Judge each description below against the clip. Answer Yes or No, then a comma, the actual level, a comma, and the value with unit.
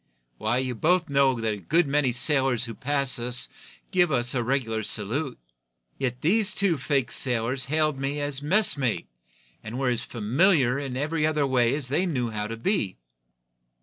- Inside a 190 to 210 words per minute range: No, average, 175 wpm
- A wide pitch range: No, average, 3.8 semitones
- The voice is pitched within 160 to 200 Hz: No, low, 135 Hz